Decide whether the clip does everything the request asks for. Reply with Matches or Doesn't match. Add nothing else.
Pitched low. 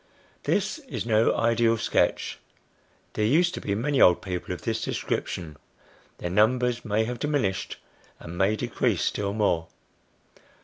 Matches